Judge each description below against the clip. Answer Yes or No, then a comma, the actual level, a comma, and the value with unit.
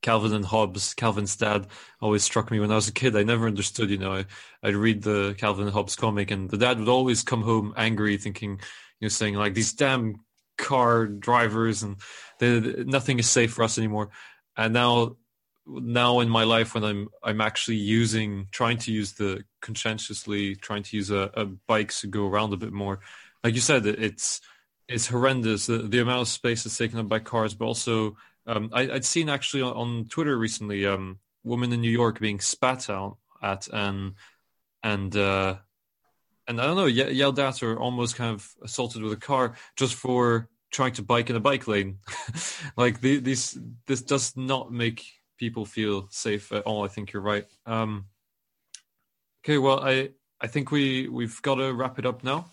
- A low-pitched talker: Yes, low, 115 Hz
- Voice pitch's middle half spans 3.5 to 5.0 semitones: No, average, 2.9 semitones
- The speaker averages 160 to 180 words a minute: No, average, 200 wpm